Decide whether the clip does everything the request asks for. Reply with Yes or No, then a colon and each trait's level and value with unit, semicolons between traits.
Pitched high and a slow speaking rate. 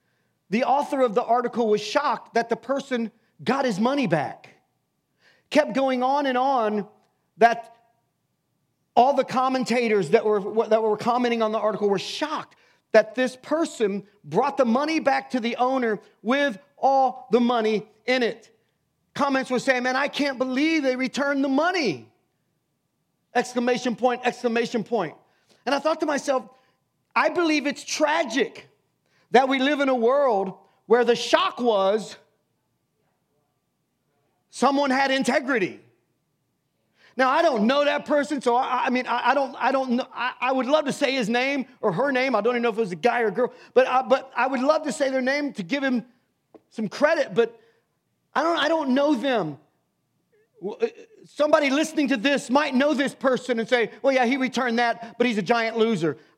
No: very high, 255 Hz; average, 180 wpm